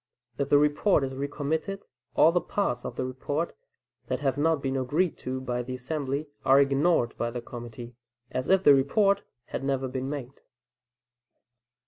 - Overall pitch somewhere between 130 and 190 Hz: Yes, medium, 140 Hz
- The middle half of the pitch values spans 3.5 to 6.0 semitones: No, average, 3.1 semitones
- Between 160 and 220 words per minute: Yes, average, 165 wpm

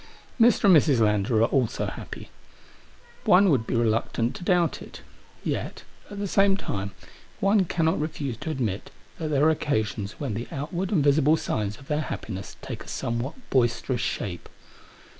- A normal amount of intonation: No, wide, 6.4 semitones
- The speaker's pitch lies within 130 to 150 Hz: Yes, medium, 140 Hz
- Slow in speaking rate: No, average, 165 wpm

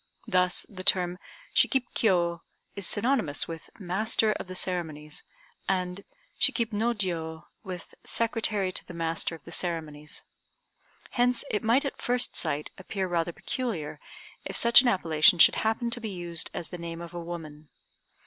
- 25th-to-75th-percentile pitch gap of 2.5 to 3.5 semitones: No, average, 4.8 semitones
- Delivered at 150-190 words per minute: Yes, average, 160 wpm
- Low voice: No, medium, 180 Hz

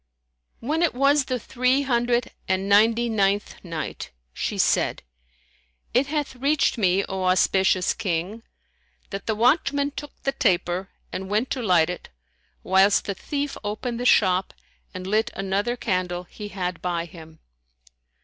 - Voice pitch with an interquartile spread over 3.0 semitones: Yes, average, 5.2 semitones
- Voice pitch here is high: Yes, high, 205 Hz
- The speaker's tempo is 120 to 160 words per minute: Yes, average, 145 wpm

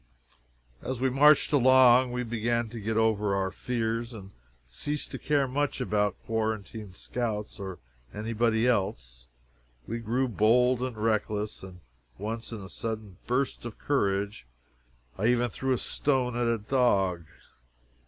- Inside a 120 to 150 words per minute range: Yes, average, 145 wpm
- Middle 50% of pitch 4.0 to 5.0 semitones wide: No, average, 3.1 semitones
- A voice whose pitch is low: Yes, low, 115 Hz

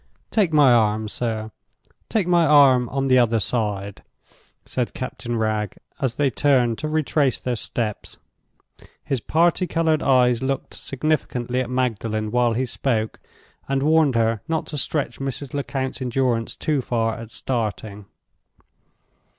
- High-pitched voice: No, low, 125 Hz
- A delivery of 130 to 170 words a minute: Yes, slow, 135 wpm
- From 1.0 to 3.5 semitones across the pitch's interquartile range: No, average, 3.9 semitones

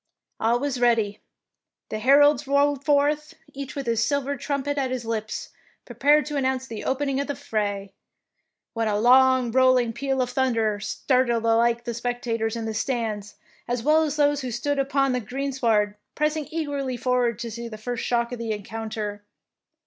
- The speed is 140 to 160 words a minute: No, average, 170 wpm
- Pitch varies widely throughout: No, average, 3.6 semitones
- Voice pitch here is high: Yes, very high, 250 Hz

